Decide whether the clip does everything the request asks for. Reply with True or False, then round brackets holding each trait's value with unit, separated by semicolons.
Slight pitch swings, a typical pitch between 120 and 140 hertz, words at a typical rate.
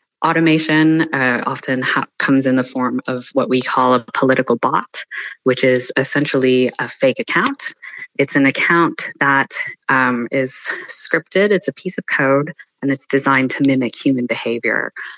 True (2.2 semitones; 135 Hz; 160 wpm)